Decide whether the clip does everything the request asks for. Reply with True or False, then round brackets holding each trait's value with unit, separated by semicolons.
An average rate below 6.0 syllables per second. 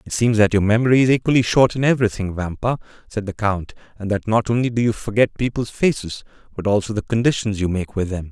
False (6.3 syllables/s)